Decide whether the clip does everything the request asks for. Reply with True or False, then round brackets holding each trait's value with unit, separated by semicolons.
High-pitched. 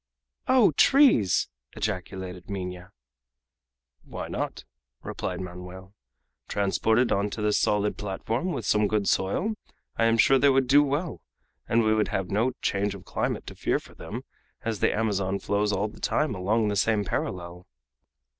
False (105 Hz)